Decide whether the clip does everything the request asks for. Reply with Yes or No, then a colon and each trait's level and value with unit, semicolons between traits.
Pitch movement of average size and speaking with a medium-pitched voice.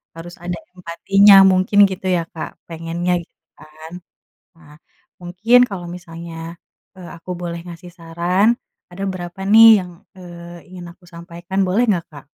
No: narrow, 1.6 semitones; medium, 175 Hz